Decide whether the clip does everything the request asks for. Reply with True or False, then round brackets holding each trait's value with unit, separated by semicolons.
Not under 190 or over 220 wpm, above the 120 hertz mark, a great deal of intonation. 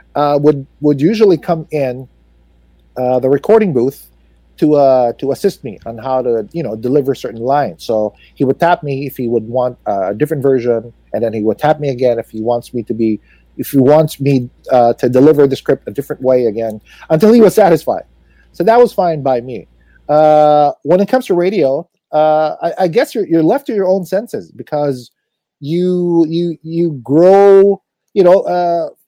True (200 wpm; 140 Hz; 5.7 semitones)